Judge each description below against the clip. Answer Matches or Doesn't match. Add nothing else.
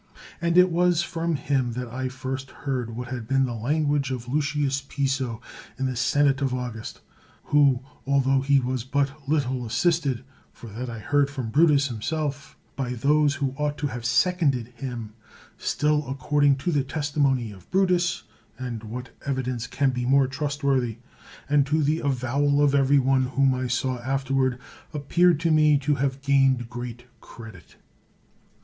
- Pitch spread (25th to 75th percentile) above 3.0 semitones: Doesn't match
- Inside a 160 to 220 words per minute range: Matches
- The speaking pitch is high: Doesn't match